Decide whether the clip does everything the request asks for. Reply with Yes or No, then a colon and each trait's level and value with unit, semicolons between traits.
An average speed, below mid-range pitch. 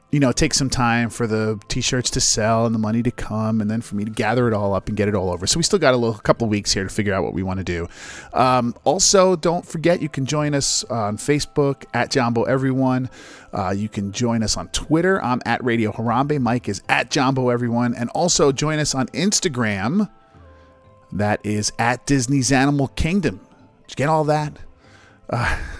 No: fast, 220 wpm; low, 120 Hz